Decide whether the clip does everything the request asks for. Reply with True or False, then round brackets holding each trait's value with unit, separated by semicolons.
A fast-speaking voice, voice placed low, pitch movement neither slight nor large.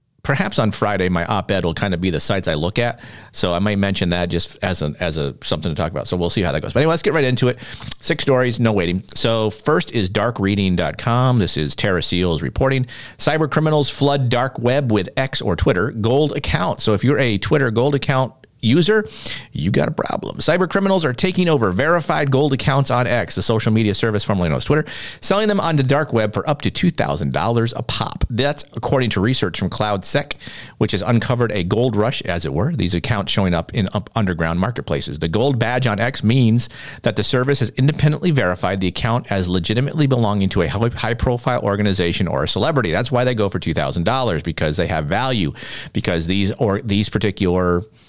False (210 wpm; 115 Hz; 5.9 semitones)